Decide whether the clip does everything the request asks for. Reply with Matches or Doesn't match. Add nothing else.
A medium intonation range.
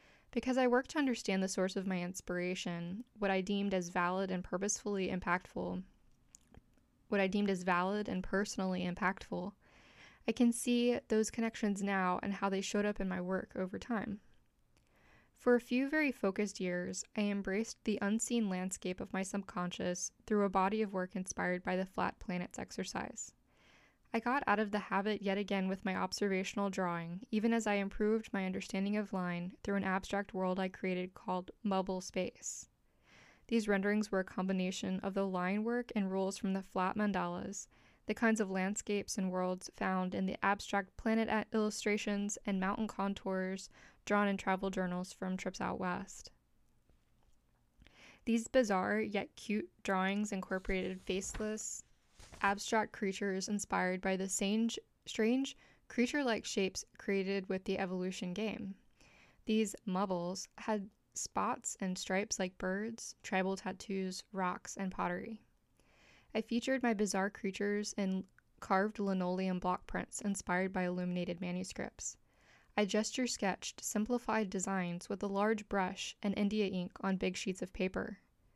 Doesn't match